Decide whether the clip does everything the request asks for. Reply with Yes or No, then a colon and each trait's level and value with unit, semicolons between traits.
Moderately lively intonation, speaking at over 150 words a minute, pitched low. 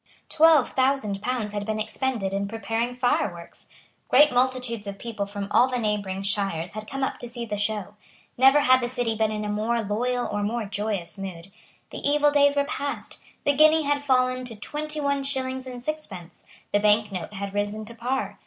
No: average, 4.2 semitones; average, 195 wpm; high, 230 Hz